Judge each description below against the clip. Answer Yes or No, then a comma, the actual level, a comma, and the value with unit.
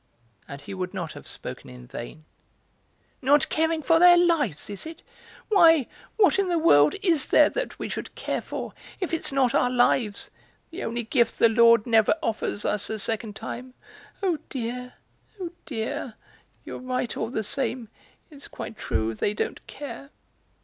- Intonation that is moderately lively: No, wide, 6.5 semitones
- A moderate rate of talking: Yes, average, 170 wpm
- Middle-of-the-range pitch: No, very high, 250 Hz